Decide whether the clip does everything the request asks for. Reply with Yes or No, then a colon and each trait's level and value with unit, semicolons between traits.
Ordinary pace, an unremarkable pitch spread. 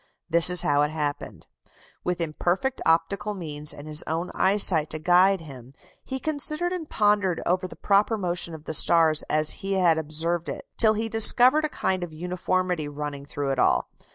Yes: average, 180 wpm; average, 4.3 semitones